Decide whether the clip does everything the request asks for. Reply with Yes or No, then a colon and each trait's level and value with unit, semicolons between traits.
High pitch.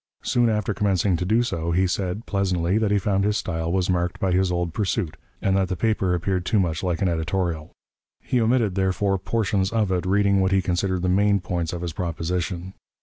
No: very low, 95 Hz